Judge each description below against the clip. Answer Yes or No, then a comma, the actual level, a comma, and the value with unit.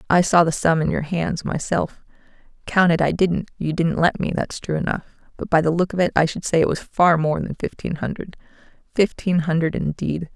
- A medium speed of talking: No, fast, 210 wpm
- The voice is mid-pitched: Yes, medium, 165 Hz